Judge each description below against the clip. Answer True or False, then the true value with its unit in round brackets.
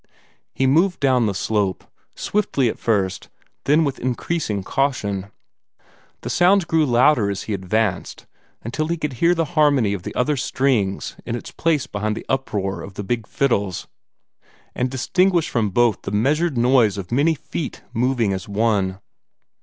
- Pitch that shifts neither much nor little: False (6.2 semitones)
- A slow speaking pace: False (160 wpm)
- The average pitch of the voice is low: True (120 Hz)